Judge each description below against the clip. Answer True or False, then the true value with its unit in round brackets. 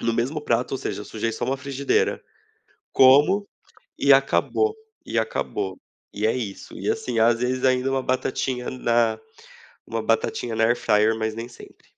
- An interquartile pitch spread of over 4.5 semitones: False (2.6 semitones)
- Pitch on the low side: True (120 Hz)